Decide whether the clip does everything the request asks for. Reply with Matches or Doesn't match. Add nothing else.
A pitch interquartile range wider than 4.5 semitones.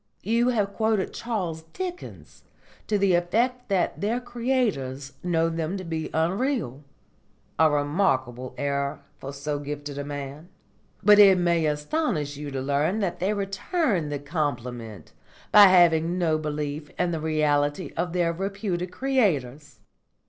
Matches